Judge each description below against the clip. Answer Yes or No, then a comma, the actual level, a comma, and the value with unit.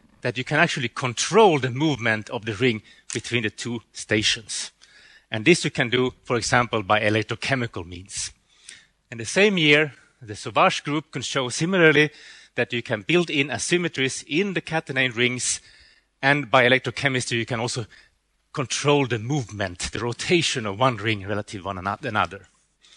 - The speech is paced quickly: No, average, 160 wpm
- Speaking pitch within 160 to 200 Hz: No, low, 125 Hz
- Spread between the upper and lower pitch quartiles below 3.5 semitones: No, average, 4.3 semitones